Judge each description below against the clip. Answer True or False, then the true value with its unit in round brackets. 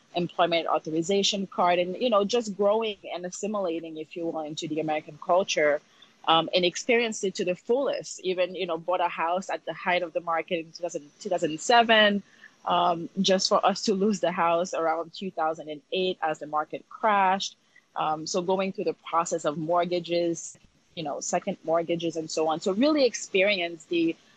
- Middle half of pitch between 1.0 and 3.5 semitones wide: True (2.9 semitones)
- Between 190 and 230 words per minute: False (175 wpm)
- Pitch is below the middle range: False (175 Hz)